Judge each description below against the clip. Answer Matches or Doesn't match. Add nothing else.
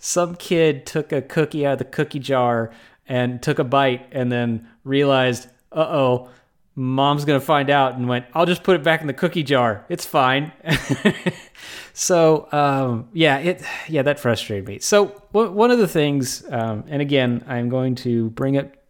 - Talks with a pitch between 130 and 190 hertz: Matches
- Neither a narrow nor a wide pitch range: Matches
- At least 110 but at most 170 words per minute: Doesn't match